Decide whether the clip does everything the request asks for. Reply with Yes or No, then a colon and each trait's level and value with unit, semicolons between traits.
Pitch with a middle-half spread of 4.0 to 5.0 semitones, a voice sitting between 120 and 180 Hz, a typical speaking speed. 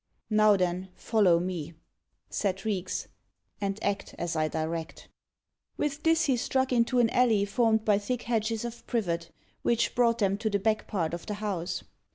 No: average, 4.3 semitones; high, 210 Hz; average, 170 wpm